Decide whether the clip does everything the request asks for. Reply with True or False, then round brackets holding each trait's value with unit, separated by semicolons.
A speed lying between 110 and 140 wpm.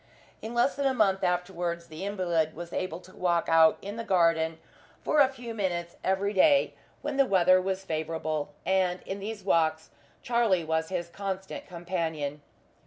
False (170 wpm)